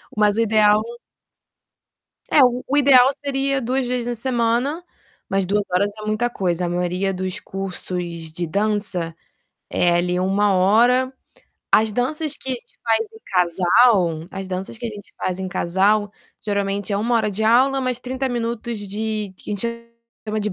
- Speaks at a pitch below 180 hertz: No, high, 210 Hz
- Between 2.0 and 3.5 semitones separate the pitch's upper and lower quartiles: No, average, 4.2 semitones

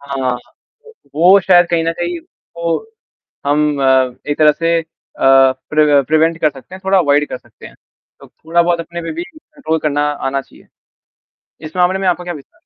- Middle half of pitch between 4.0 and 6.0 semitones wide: No, average, 3.3 semitones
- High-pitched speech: No, medium, 165 Hz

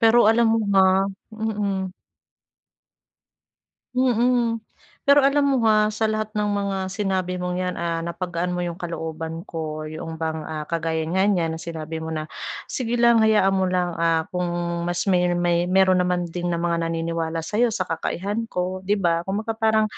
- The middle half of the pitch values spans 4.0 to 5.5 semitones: Yes, average, 4.3 semitones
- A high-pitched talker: No, medium, 180 Hz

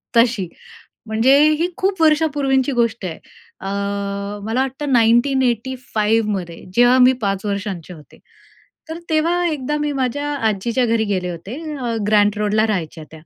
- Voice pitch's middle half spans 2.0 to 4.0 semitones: No, average, 4.6 semitones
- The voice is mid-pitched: No, high, 235 Hz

